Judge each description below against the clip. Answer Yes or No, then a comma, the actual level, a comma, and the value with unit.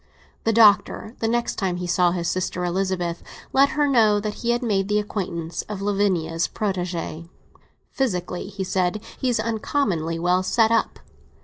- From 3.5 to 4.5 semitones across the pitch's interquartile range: Yes, average, 3.8 semitones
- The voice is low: No, high, 195 Hz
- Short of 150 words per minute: No, average, 155 wpm